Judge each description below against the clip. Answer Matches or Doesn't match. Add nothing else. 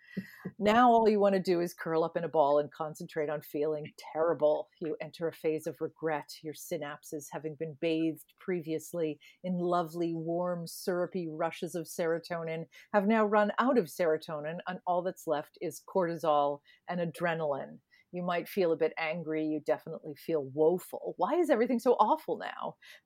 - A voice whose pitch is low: Doesn't match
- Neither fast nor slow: Matches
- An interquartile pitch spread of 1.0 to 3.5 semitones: Matches